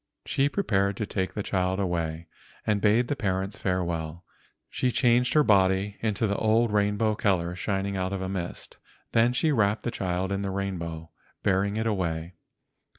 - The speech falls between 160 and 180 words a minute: Yes, average, 170 wpm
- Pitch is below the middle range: Yes, low, 100 Hz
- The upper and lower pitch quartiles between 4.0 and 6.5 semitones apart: No, average, 2.8 semitones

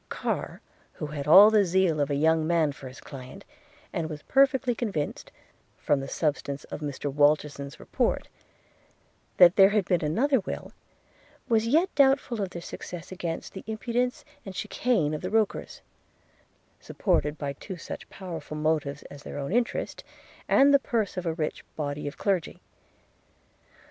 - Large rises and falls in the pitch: Yes, wide, 6.6 semitones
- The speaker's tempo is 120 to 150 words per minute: No, average, 160 wpm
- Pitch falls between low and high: Yes, medium, 170 Hz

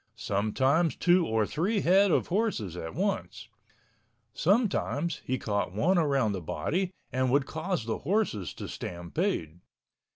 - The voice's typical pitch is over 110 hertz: Yes, medium, 140 Hz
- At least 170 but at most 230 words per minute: No, slow, 135 wpm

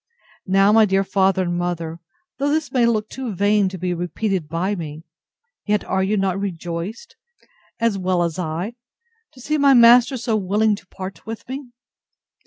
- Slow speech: No, average, 175 wpm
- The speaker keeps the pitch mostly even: No, average, 4.1 semitones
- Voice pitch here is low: No, high, 195 Hz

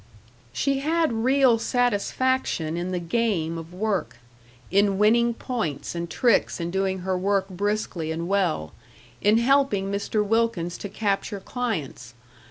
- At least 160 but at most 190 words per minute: No, slow, 135 wpm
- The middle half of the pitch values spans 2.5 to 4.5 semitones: No, average, 4.9 semitones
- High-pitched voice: Yes, high, 200 Hz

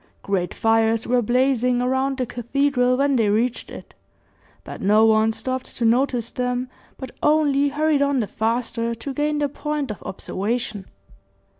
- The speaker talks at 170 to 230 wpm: No, average, 155 wpm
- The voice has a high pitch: Yes, very high, 250 Hz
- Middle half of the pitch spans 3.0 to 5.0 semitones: Yes, average, 3.5 semitones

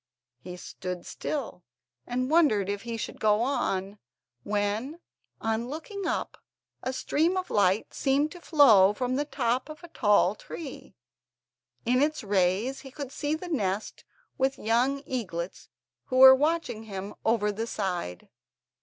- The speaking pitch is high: Yes, high, 240 Hz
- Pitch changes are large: Yes, wide, 5.7 semitones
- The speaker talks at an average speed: Yes, average, 150 wpm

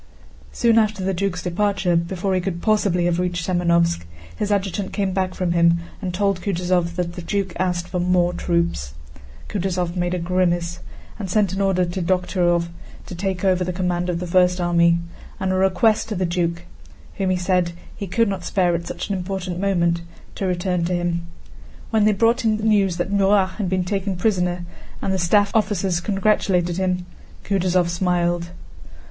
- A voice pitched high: No, medium, 180 Hz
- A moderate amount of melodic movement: No, narrow, 1.9 semitones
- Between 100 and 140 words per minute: No, average, 175 wpm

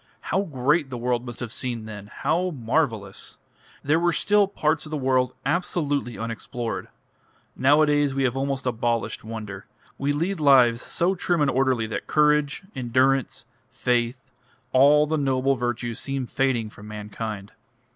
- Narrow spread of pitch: No, average, 3.9 semitones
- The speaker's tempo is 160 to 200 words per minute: No, average, 145 wpm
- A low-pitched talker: Yes, low, 130 Hz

